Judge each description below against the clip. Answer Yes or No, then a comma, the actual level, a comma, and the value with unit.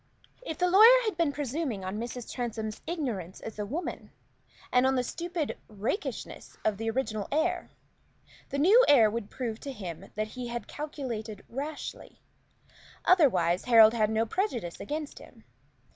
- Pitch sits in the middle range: No, high, 245 Hz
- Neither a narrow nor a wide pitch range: No, wide, 6.1 semitones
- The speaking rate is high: No, average, 155 wpm